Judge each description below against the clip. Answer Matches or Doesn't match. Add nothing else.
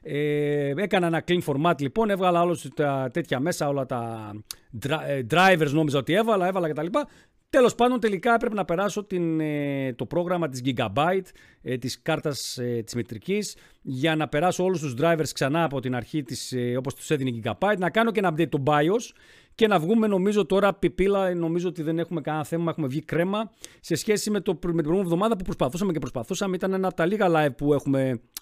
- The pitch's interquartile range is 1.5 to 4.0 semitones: Doesn't match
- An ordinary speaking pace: Doesn't match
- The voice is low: Doesn't match